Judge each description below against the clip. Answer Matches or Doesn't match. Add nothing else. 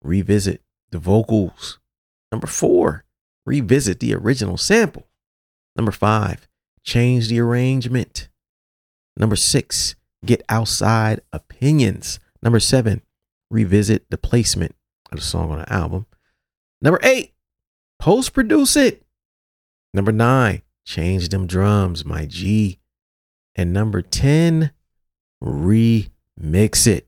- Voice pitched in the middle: Doesn't match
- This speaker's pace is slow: Matches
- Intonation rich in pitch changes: Matches